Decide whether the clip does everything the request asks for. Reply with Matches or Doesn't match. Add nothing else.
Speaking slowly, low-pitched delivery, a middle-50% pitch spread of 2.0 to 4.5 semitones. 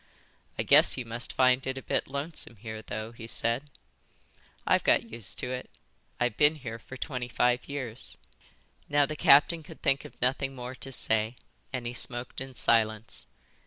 Doesn't match